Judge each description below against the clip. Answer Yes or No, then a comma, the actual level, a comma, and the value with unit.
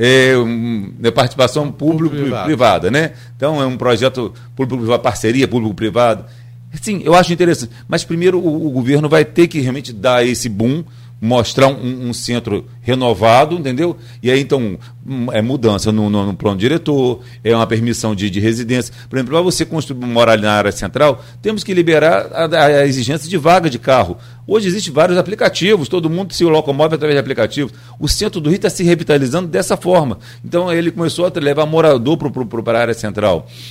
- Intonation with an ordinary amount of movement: Yes, average, 5.0 semitones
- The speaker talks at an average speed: Yes, average, 175 wpm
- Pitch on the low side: Yes, low, 130 Hz